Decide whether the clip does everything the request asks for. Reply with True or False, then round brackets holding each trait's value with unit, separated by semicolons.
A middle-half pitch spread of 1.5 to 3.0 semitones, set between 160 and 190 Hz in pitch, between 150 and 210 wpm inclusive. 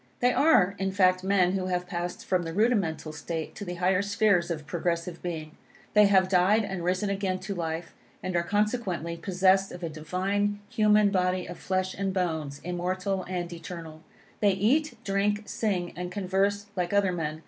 True (2.5 semitones; 185 Hz; 180 wpm)